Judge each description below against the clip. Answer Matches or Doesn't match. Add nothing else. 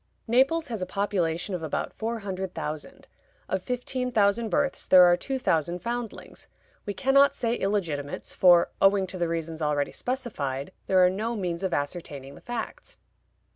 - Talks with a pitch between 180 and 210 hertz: Matches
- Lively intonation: Matches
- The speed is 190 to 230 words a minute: Doesn't match